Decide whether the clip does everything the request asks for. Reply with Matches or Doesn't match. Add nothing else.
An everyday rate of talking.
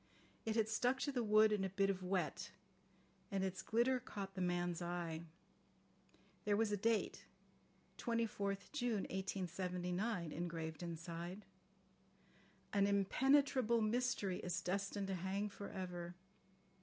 Doesn't match